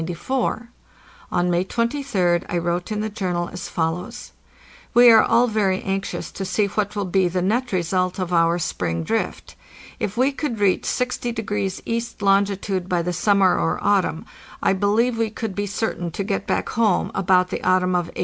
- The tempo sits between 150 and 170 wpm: No, average, 185 wpm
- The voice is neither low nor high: No, high, 195 Hz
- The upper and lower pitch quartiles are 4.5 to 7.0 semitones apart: No, average, 3.3 semitones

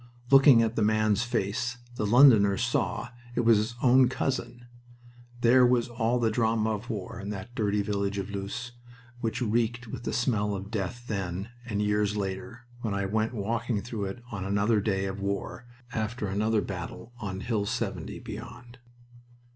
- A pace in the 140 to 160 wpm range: No, average, 170 wpm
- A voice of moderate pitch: No, low, 110 Hz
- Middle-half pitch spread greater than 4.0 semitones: No, average, 3.0 semitones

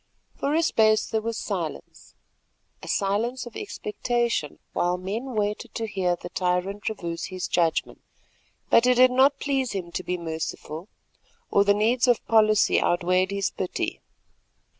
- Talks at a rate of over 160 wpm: No, average, 150 wpm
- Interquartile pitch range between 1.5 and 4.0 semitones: No, average, 4.7 semitones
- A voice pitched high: Yes, high, 205 Hz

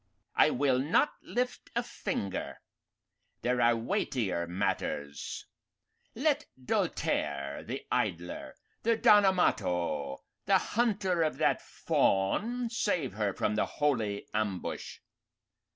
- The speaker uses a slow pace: Yes, slow, 105 wpm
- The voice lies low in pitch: Yes, low, 125 Hz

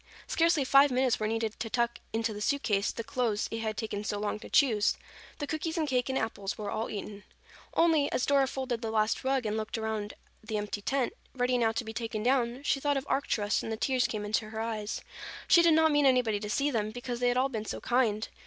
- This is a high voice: Yes, high, 235 Hz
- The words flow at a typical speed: No, fast, 240 wpm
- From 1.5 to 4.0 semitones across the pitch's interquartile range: Yes, average, 3.7 semitones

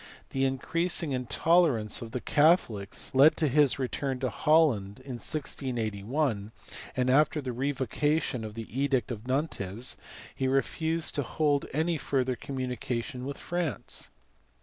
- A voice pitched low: Yes, low, 130 Hz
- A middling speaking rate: No, slow, 130 wpm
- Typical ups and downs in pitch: Yes, average, 3.9 semitones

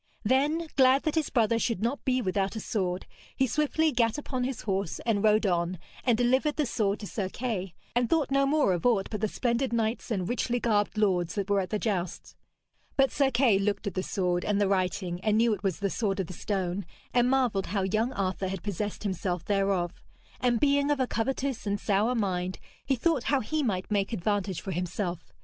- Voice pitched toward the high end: Yes, high, 210 Hz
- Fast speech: Yes, fast, 215 wpm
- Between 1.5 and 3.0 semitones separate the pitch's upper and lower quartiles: No, average, 4.6 semitones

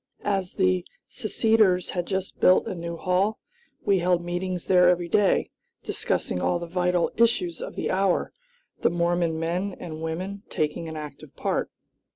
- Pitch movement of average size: No, narrow, 1.9 semitones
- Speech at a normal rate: Yes, average, 160 wpm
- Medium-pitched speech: Yes, medium, 180 Hz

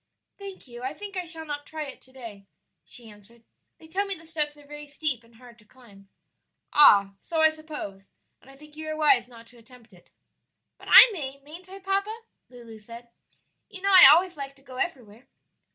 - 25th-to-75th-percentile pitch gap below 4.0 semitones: No, average, 5.3 semitones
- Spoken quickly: Yes, fast, 210 wpm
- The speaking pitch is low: No, very high, 280 Hz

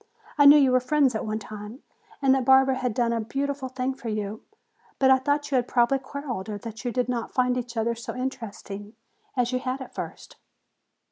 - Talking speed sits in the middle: No, fast, 215 wpm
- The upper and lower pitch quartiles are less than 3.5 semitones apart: Yes, average, 2.7 semitones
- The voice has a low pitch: No, very high, 250 Hz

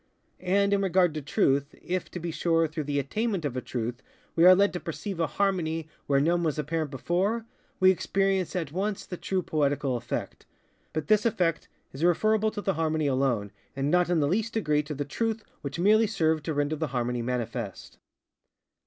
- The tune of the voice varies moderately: Yes, average, 4.8 semitones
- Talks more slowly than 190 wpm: No, average, 195 wpm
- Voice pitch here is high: No, medium, 165 Hz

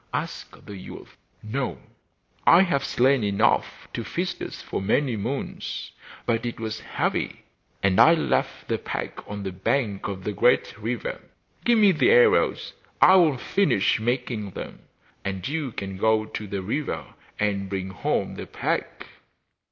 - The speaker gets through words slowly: No, average, 155 wpm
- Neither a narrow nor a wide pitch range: No, wide, 5.9 semitones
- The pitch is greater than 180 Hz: No, low, 110 Hz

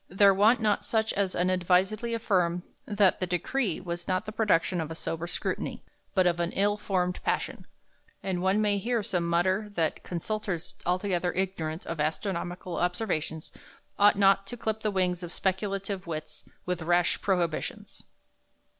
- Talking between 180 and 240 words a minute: No, average, 155 wpm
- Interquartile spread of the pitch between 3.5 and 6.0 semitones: No, average, 2.8 semitones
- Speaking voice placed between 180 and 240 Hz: Yes, medium, 185 Hz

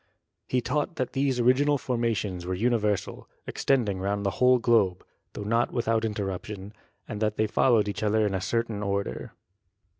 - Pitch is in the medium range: No, low, 110 Hz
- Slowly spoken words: No, average, 175 wpm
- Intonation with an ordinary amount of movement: Yes, average, 3.3 semitones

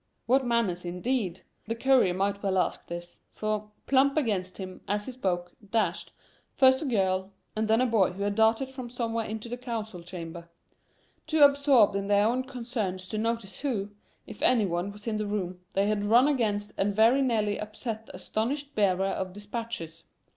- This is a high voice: Yes, high, 215 Hz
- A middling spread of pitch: Yes, average, 3.9 semitones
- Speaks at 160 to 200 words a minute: Yes, average, 185 wpm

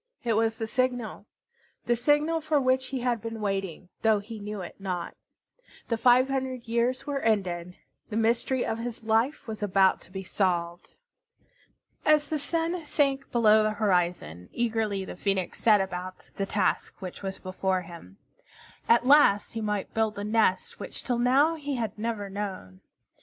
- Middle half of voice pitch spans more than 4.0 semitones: Yes, average, 4.6 semitones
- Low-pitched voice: No, high, 220 Hz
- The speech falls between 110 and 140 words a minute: No, average, 170 wpm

